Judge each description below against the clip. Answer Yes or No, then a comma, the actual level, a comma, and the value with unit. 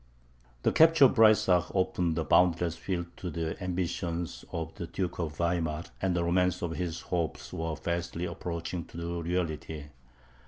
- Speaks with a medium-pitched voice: No, very low, 85 Hz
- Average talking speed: Yes, average, 155 wpm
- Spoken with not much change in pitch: Yes, narrow, 1.5 semitones